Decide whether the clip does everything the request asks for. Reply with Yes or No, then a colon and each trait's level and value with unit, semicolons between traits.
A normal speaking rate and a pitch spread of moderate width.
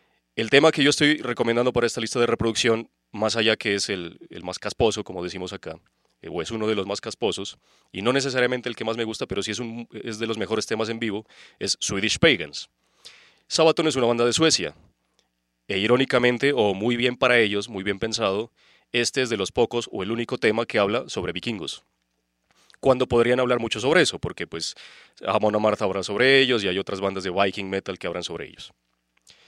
No: fast, 215 wpm; average, 3.7 semitones